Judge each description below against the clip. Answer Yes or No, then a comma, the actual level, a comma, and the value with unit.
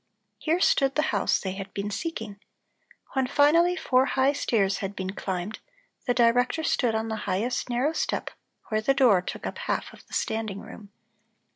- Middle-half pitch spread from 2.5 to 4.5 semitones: No, average, 5.2 semitones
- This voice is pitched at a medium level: No, high, 230 Hz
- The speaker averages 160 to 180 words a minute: Yes, average, 175 wpm